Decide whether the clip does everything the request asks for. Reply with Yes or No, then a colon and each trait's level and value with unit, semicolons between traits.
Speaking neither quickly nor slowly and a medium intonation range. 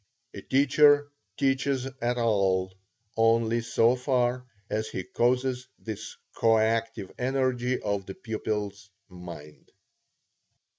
No: slow, 100 wpm; average, 3.6 semitones